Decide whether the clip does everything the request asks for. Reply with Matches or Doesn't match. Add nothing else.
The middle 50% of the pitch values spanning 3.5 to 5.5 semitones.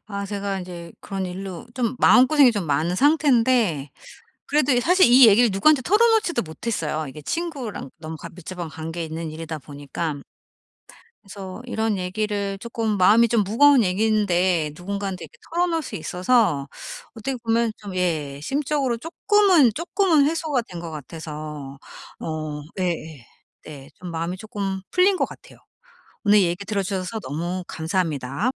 Doesn't match